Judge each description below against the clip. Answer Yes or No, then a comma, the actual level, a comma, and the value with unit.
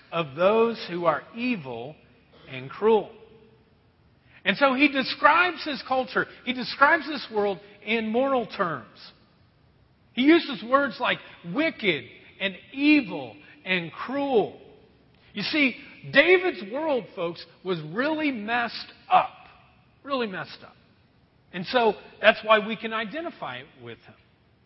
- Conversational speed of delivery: No, slow, 125 wpm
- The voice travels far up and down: Yes, wide, 8.3 semitones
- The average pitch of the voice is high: Yes, high, 220 Hz